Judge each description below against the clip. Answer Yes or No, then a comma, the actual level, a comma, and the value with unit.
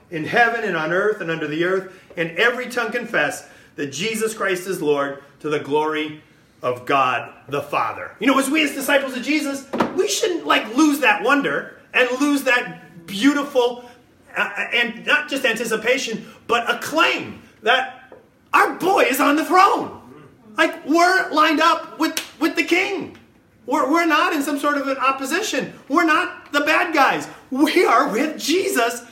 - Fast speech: No, average, 175 wpm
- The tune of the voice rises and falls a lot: Yes, wide, 6.7 semitones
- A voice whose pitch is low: No, very high, 260 Hz